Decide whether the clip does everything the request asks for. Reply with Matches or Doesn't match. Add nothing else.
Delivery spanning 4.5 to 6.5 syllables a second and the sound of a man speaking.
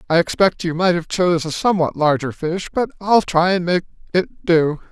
Matches